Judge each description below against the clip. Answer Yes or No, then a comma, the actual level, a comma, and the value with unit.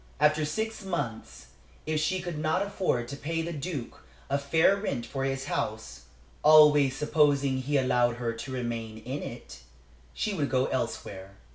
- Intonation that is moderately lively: Yes, average, 4.3 semitones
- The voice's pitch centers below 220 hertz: Yes, medium, 140 Hz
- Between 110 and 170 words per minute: Yes, average, 160 wpm